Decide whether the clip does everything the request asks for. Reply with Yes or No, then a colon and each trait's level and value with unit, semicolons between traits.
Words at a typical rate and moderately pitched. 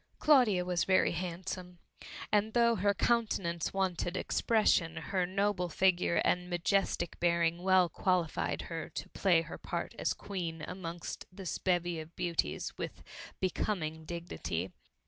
No: slow, 130 wpm; medium, 180 Hz